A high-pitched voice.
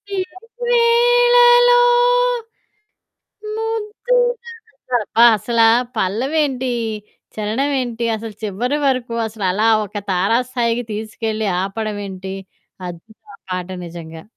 Yes: high, 235 Hz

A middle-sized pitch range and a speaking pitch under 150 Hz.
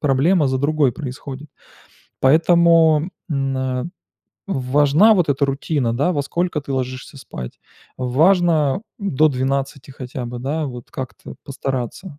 Yes: average, 3.2 semitones; medium, 140 Hz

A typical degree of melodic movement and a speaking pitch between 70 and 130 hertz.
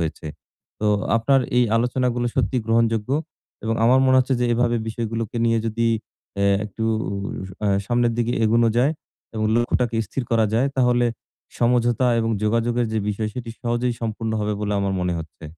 No: narrow, 1.7 semitones; low, 115 Hz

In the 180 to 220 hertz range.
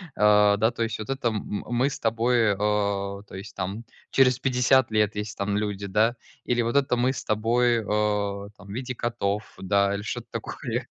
No: low, 105 Hz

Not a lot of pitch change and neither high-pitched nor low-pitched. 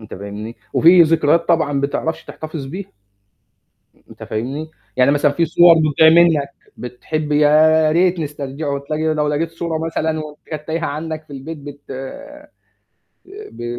Yes: narrow, 2.3 semitones; medium, 155 Hz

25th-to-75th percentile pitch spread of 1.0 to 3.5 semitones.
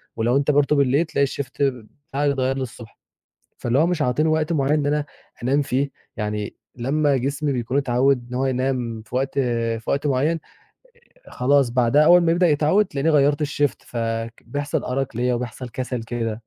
Yes: average, 2.9 semitones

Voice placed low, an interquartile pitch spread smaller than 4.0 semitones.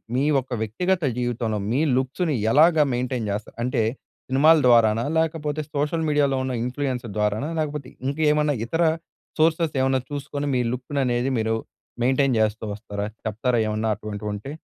No: low, 130 Hz; average, 4.6 semitones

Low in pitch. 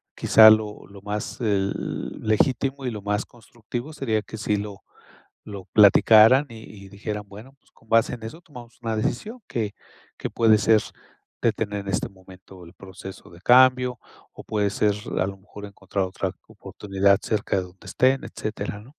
Yes: low, 105 Hz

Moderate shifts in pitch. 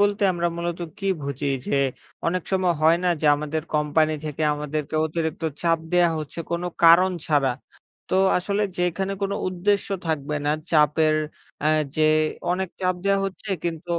Yes: average, 3.1 semitones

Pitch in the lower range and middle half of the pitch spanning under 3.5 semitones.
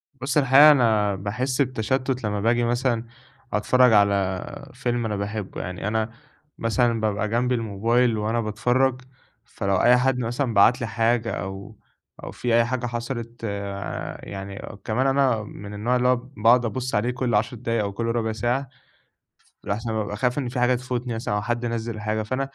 Yes: low, 115 Hz; average, 2.8 semitones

